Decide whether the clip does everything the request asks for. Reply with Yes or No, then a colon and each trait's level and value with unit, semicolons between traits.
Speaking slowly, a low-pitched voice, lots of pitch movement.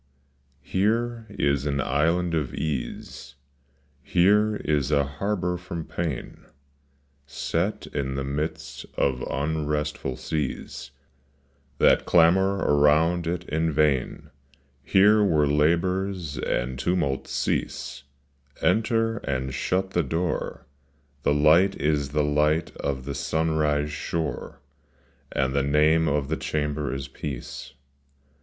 No: slow, 110 wpm; very low, 75 Hz; average, 3.6 semitones